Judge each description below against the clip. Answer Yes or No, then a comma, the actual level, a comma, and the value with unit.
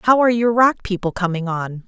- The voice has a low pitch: No, high, 205 Hz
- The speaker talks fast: Yes, fast, 225 wpm